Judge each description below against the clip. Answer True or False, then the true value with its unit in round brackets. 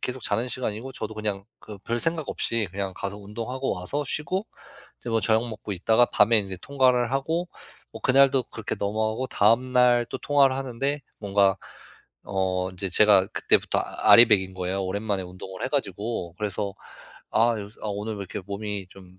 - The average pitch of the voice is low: True (110 Hz)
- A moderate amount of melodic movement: True (4.3 semitones)